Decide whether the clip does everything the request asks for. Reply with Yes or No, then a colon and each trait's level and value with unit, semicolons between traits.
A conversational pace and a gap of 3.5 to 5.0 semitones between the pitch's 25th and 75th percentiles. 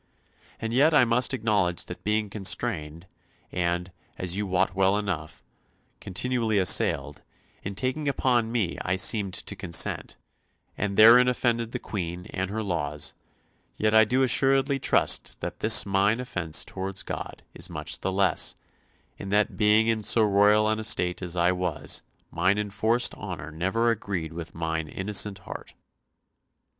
Yes: average, 150 wpm; average, 4.0 semitones